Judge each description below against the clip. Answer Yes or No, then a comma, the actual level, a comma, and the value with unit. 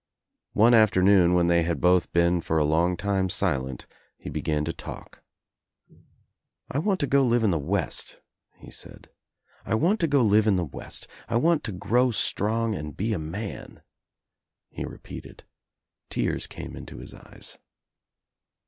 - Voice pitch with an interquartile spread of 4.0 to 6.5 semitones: Yes, average, 5.1 semitones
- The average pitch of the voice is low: Yes, low, 100 Hz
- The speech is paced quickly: No, average, 160 wpm